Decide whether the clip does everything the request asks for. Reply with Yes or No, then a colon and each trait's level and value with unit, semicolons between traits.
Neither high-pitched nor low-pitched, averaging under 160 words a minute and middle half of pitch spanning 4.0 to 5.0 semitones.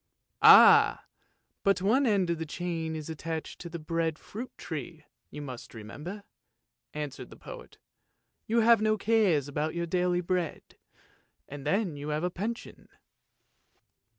Yes: medium, 170 Hz; average, 150 wpm; average, 4.7 semitones